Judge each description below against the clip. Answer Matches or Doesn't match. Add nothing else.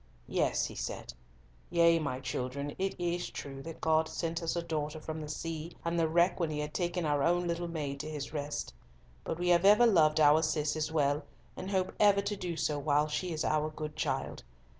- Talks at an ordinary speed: Doesn't match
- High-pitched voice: Doesn't match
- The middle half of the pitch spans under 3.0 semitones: Matches